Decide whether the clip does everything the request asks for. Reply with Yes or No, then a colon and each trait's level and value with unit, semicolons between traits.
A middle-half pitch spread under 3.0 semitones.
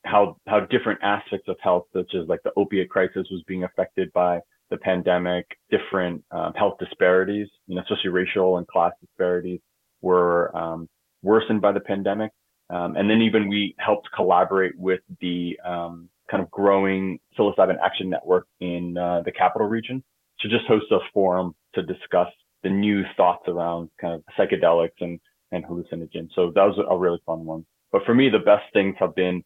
Yes: narrow, 2.4 semitones